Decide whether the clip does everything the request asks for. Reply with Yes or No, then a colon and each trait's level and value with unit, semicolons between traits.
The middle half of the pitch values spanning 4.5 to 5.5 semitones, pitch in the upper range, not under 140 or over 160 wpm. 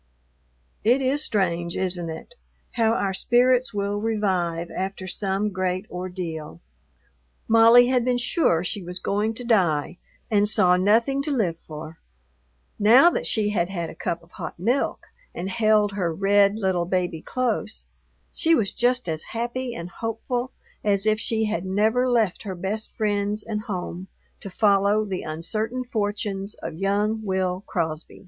No: average, 3.8 semitones; high, 205 Hz; average, 155 wpm